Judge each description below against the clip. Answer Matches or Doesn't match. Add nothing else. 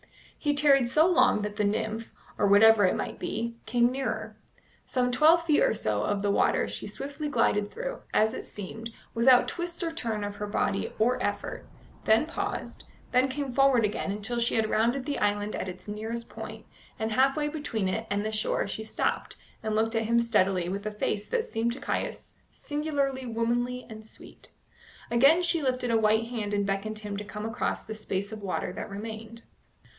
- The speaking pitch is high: Matches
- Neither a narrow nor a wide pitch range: Matches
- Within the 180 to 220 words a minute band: Matches